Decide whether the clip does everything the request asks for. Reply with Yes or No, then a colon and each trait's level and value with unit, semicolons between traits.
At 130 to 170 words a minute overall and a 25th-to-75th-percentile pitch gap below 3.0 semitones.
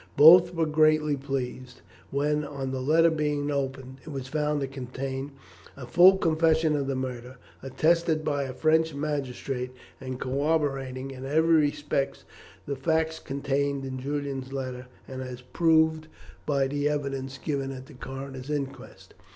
Yes: average, 150 wpm; narrow, 2.6 semitones